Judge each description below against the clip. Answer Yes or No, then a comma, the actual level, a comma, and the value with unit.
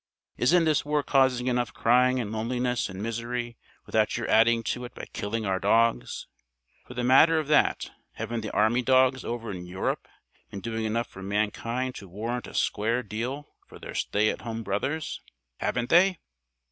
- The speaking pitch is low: Yes, low, 120 Hz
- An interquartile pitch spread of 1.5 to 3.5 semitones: Yes, average, 2.8 semitones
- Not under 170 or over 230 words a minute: Yes, average, 175 wpm